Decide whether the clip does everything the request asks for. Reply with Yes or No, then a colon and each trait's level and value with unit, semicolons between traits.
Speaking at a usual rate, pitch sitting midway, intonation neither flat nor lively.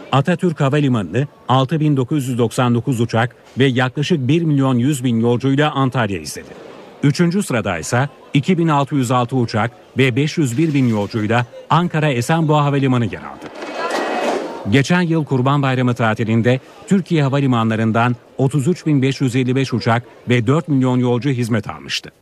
No: average, 105 wpm; low, 130 Hz; average, 3.5 semitones